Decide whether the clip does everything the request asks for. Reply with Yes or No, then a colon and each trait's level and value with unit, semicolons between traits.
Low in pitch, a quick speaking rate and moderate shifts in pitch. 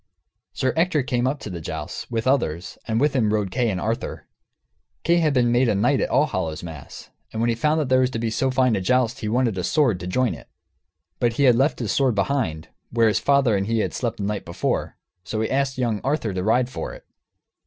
Yes: low, 120 Hz; fast, 235 wpm; average, 3.9 semitones